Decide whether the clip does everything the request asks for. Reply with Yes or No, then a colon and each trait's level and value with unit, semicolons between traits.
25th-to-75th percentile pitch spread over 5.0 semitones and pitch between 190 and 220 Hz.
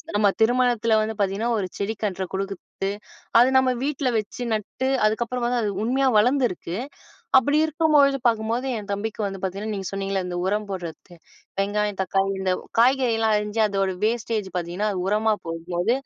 No: average, 3.6 semitones; high, 215 Hz